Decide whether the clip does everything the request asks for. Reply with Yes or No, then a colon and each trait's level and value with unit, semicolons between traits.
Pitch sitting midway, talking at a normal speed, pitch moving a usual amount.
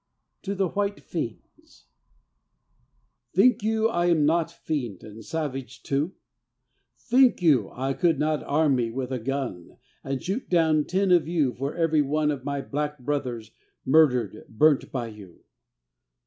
Yes: medium, 150 Hz; average, 150 wpm; average, 4.8 semitones